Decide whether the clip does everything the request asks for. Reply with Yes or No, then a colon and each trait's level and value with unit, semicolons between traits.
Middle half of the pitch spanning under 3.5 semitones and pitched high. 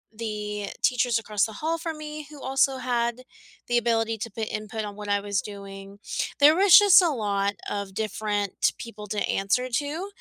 No: average, 4.7 semitones; high, 225 Hz